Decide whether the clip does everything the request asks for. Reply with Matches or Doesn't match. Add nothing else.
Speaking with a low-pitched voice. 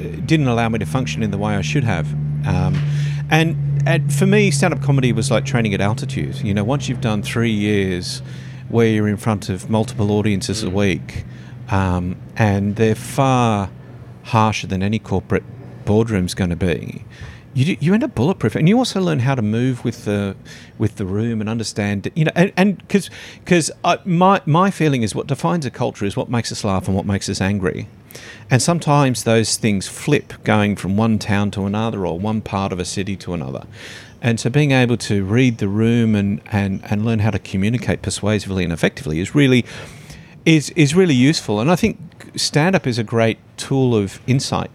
Matches